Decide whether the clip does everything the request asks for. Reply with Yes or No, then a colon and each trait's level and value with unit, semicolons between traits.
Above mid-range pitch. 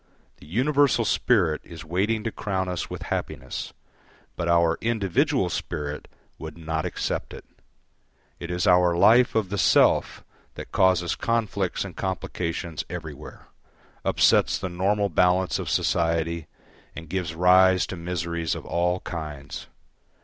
No: very low, 90 Hz